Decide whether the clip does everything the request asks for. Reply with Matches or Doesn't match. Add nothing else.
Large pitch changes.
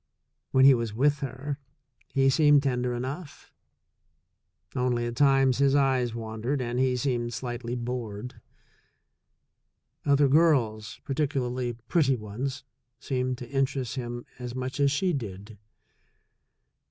Doesn't match